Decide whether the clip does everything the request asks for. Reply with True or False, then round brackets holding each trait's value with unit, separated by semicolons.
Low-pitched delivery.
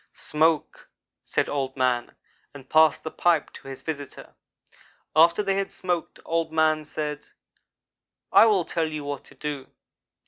False (155 Hz)